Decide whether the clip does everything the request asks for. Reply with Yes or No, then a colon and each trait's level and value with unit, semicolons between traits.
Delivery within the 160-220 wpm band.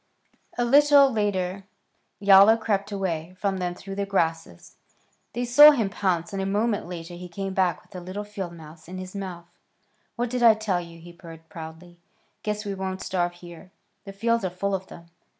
Yes: average, 190 wpm